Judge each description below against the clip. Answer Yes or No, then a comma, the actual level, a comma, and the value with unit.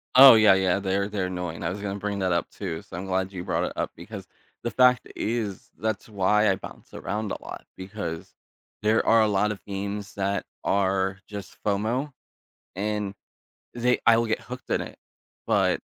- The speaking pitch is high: No, low, 100 Hz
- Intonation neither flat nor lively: No, narrow, 2.3 semitones